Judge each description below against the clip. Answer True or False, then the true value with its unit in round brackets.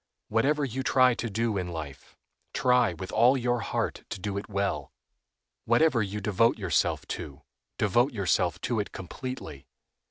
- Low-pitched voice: True (105 Hz)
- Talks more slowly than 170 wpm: True (155 wpm)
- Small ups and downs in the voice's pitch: False (4.8 semitones)